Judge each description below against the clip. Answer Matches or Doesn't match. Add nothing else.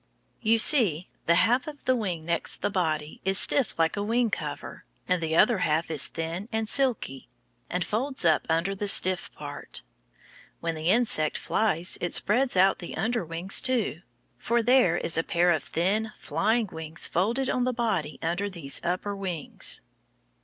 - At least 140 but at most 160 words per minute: Doesn't match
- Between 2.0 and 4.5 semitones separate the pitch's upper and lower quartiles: Doesn't match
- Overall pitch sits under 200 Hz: Matches